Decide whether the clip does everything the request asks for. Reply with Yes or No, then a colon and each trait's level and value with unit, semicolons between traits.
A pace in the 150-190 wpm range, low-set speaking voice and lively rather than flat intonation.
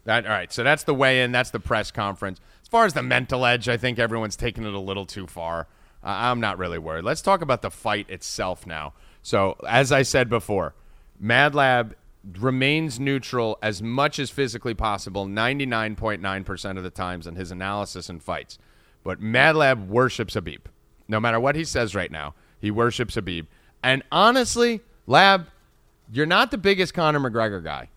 Yes: average, 185 wpm; low, 115 Hz; wide, 5.8 semitones